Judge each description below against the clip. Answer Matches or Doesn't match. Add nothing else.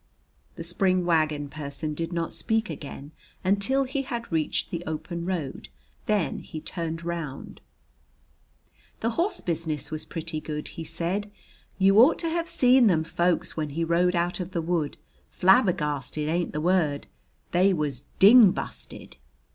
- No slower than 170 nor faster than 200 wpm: Doesn't match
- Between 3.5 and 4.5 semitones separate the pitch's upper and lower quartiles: Matches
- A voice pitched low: Doesn't match